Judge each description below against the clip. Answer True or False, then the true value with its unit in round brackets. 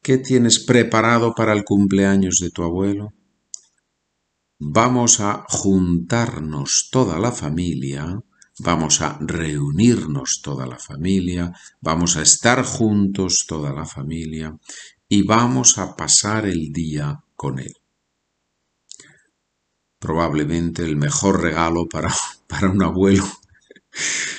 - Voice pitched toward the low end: True (85 Hz)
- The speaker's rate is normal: False (110 wpm)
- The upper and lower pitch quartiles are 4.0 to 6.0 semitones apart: True (5.0 semitones)